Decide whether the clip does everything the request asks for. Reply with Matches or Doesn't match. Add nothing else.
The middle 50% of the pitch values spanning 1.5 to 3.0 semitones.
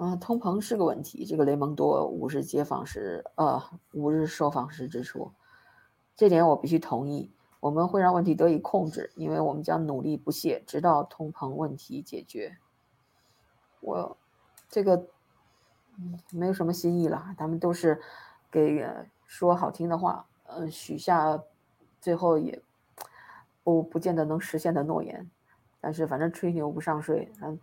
Matches